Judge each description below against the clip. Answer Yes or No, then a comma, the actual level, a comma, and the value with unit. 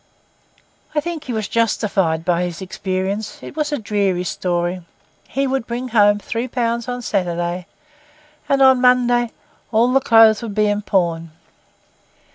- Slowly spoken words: No, average, 150 wpm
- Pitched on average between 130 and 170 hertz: No, high, 215 Hz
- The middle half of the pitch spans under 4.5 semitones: No, average, 5.0 semitones